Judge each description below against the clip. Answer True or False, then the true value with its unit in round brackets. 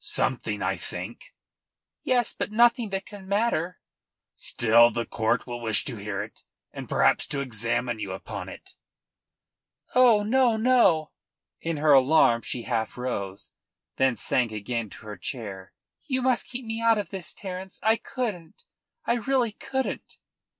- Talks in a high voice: False (160 Hz)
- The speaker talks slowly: False (150 wpm)